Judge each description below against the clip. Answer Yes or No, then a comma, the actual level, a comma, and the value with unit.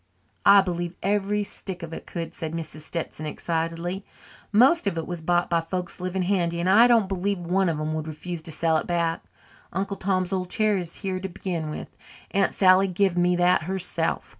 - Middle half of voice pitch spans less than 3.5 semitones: Yes, narrow, 2.5 semitones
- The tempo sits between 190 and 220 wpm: Yes, average, 200 wpm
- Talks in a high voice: No, medium, 180 Hz